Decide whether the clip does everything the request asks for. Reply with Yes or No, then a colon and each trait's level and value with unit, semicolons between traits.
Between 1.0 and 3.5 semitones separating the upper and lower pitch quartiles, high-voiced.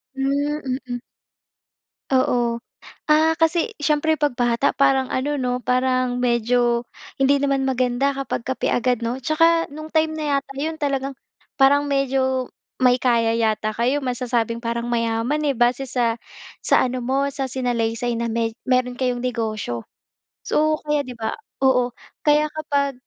Yes: average, 2.8 semitones; very high, 255 Hz